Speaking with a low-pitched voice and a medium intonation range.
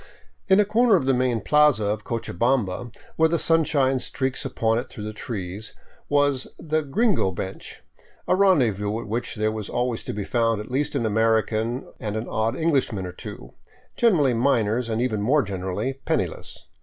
Yes: low, 120 Hz; average, 4.9 semitones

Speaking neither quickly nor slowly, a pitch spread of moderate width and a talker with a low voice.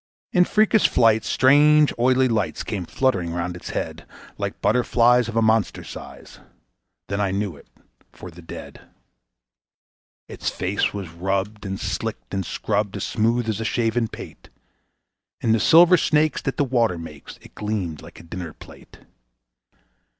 Yes: average, 155 wpm; average, 4.6 semitones; low, 110 Hz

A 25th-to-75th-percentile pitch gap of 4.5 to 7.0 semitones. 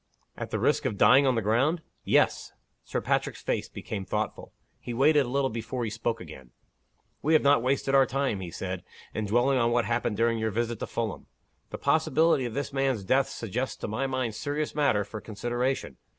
No: average, 3.7 semitones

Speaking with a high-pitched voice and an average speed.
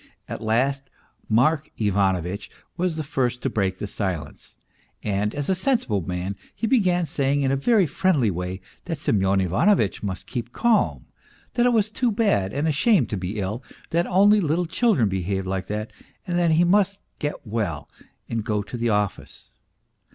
No: low, 125 Hz; average, 175 wpm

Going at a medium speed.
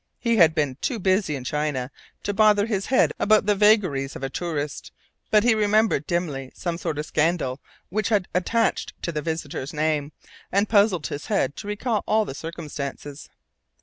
Yes: average, 180 wpm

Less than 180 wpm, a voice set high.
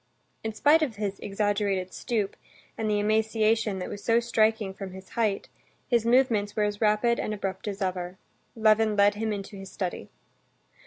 Yes: average, 170 wpm; high, 210 Hz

